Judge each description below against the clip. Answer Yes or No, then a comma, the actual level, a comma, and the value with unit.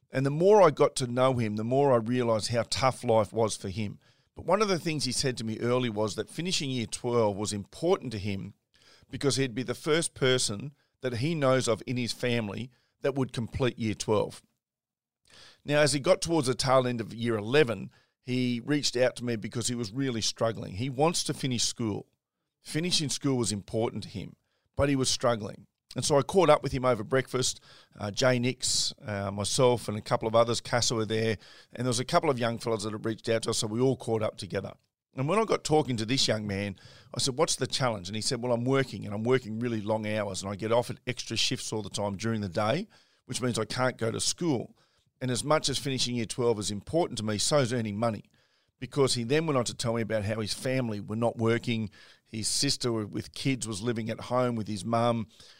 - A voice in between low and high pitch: No, low, 120 Hz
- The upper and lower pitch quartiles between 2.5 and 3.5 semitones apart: Yes, average, 3.2 semitones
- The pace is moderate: No, fast, 235 wpm